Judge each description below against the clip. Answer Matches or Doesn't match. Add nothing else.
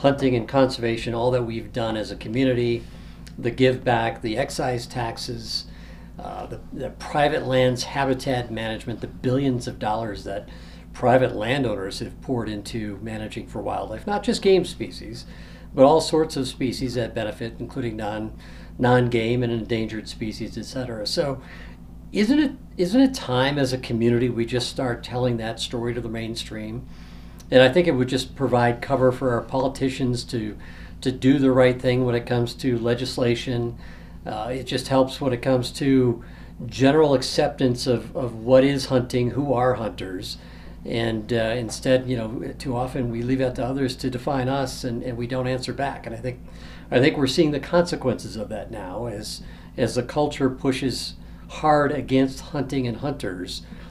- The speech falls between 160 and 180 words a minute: Matches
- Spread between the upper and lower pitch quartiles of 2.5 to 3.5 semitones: Matches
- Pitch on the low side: Matches